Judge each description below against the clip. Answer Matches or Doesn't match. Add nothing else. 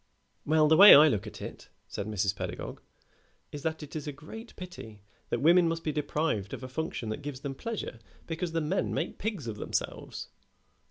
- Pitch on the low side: Doesn't match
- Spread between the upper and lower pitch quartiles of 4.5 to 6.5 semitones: Matches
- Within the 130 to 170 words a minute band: Doesn't match